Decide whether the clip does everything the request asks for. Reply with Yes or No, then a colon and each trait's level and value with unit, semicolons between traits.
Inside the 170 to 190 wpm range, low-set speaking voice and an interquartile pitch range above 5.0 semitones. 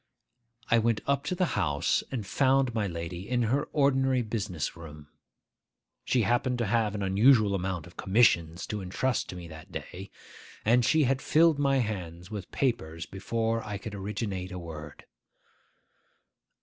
No: average, 160 wpm; low, 105 Hz; wide, 5.5 semitones